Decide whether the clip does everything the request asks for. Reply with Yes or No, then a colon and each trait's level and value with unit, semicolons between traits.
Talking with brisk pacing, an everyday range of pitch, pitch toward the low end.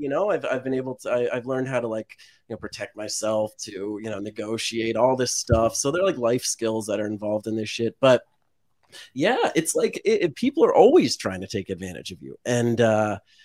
Yes: fast, 230 wpm; average, 3.4 semitones; low, 115 Hz